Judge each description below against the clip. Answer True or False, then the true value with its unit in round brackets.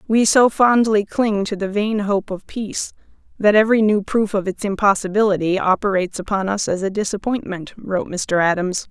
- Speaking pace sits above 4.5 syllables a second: True (5.3 syllables/s)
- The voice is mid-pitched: False (200 Hz)